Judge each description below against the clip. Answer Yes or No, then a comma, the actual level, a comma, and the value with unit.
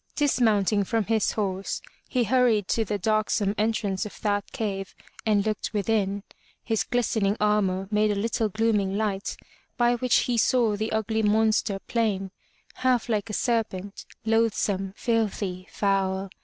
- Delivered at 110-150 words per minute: Yes, average, 145 wpm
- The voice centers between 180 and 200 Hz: No, high, 210 Hz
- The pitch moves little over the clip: Yes, narrow, 2.3 semitones